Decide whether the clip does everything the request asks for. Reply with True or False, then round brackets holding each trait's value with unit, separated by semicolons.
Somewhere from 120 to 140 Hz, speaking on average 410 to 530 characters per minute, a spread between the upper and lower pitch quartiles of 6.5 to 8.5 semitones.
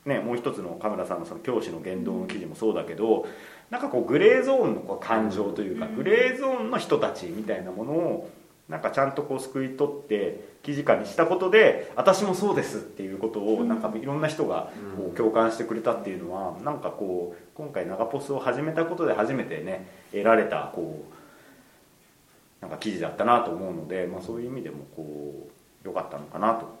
True (135 Hz; 415 characters per minute; 8.1 semitones)